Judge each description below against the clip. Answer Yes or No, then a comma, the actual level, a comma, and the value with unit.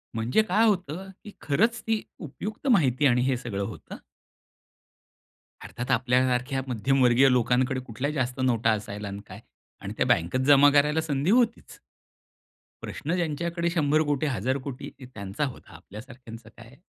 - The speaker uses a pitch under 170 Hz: Yes, low, 135 Hz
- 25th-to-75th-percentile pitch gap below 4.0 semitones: No, average, 4.4 semitones